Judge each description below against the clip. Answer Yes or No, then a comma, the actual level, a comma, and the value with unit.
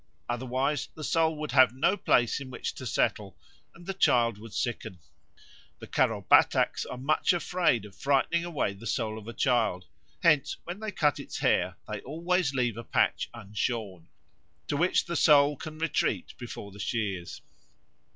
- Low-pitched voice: Yes, low, 130 Hz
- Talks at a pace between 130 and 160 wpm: No, average, 170 wpm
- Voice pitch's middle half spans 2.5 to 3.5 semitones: No, wide, 5.6 semitones